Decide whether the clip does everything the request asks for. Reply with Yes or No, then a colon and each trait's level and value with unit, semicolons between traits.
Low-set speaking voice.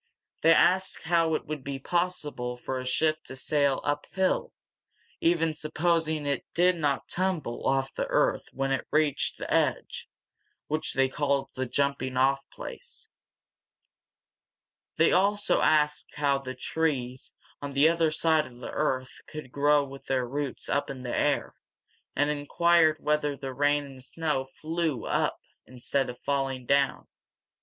No: medium, 145 Hz